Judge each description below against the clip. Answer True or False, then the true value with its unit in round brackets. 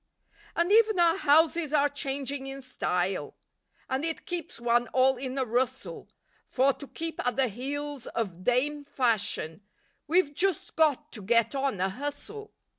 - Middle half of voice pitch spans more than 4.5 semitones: False (3.9 semitones)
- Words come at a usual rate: True (155 wpm)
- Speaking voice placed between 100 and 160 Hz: False (275 Hz)